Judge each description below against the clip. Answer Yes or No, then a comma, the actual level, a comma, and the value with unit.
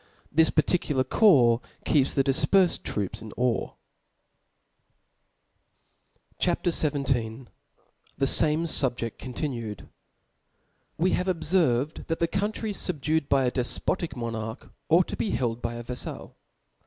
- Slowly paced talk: Yes, slow, 120 wpm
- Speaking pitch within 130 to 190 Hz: Yes, medium, 140 Hz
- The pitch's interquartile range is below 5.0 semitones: No, wide, 5.5 semitones